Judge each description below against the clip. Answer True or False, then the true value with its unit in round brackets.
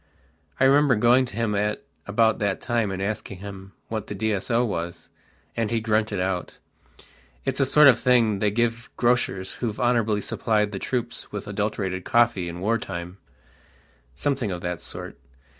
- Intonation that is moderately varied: True (3.6 semitones)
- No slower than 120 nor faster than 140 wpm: False (165 wpm)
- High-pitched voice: False (105 Hz)